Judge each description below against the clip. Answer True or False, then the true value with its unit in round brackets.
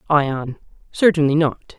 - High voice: False (150 Hz)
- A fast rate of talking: False (100 wpm)